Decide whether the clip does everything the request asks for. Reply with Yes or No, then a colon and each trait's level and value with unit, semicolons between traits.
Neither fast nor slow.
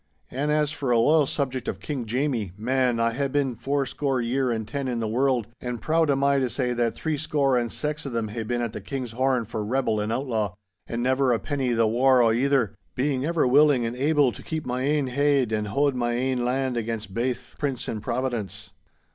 No: fast, 225 wpm